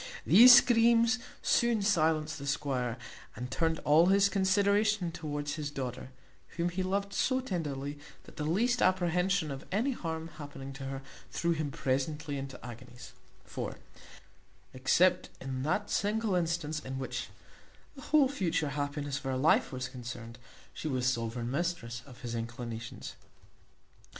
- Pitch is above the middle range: No, medium, 155 Hz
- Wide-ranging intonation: Yes, wide, 6.1 semitones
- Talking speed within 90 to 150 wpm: Yes, average, 145 wpm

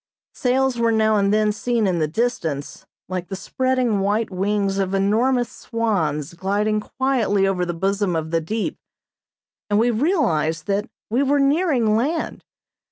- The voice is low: No, high, 210 Hz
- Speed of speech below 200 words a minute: Yes, average, 155 wpm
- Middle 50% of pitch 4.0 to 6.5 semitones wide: Yes, average, 4.3 semitones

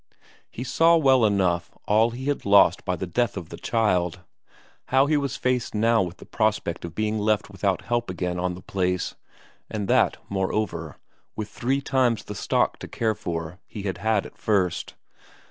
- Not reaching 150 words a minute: No, average, 180 wpm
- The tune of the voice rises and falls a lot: No, average, 4.5 semitones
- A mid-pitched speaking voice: No, low, 105 Hz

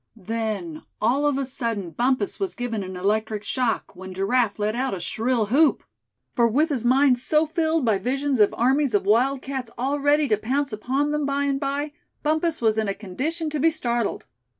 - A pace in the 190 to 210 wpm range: Yes, average, 195 wpm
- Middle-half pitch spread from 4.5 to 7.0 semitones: Yes, average, 4.8 semitones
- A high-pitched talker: Yes, very high, 250 Hz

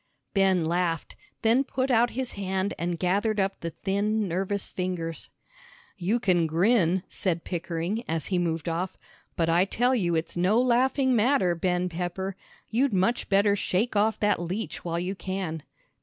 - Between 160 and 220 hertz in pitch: Yes, high, 190 Hz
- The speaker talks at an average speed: Yes, average, 160 wpm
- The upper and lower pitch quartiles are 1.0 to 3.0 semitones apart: No, average, 3.8 semitones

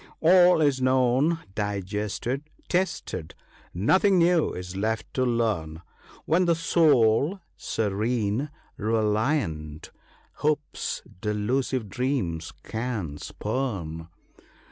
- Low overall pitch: Yes, low, 115 Hz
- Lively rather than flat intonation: Yes, wide, 6.5 semitones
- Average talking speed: No, slow, 90 wpm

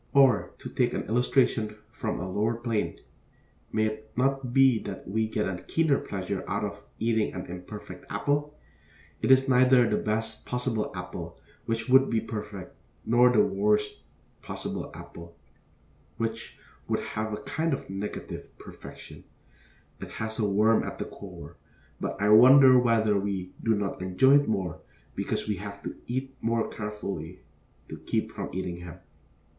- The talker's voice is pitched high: No, low, 110 Hz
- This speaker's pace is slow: No, average, 160 wpm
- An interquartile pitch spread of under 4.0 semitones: Yes, average, 3.6 semitones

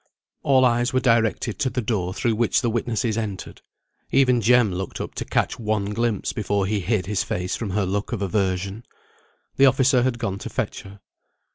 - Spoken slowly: No, average, 190 wpm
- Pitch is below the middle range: Yes, low, 110 Hz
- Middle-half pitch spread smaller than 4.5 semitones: Yes, average, 3.5 semitones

